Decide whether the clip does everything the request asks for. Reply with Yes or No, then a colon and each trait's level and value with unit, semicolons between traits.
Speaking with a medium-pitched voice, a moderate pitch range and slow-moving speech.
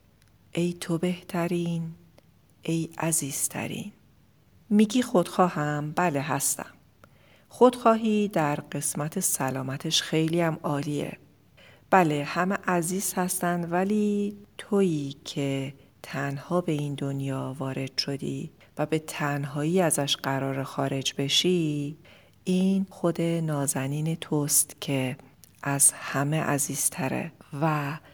Yes: medium, 155 Hz; average, 4.1 semitones; slow, 95 wpm